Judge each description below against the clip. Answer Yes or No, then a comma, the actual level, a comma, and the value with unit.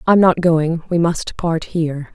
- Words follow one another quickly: No, average, 195 wpm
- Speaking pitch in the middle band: Yes, medium, 165 Hz